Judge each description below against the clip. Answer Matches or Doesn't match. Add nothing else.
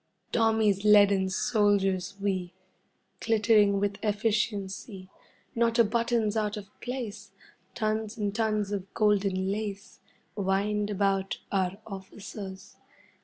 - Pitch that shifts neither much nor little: Doesn't match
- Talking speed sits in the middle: Doesn't match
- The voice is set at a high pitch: Matches